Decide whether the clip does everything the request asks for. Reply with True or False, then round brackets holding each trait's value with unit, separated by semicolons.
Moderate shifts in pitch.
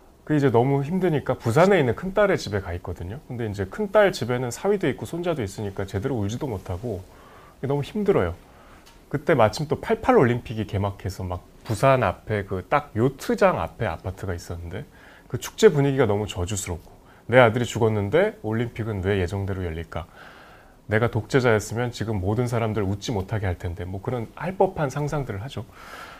False (5.9 semitones)